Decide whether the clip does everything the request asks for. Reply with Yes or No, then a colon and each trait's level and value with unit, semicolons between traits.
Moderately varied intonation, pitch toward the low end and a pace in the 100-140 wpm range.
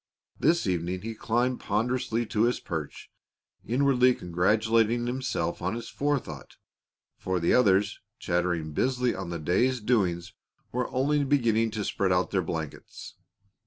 No: wide, 5.8 semitones; low, 110 Hz; slow, 135 wpm